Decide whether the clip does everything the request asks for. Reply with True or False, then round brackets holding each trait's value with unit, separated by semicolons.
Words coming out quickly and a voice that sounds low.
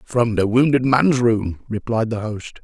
False (180 wpm; 115 Hz)